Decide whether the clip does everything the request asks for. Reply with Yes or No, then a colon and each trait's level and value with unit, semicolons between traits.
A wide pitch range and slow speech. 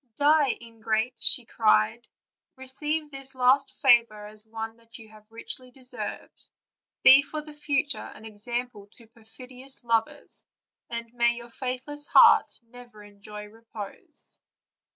No: average, 3.0 semitones; slow, 130 wpm